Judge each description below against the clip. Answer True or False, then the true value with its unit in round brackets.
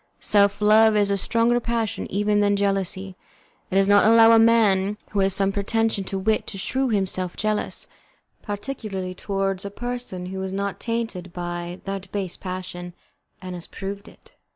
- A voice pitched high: True (200 Hz)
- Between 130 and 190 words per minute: True (170 wpm)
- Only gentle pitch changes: True (2.3 semitones)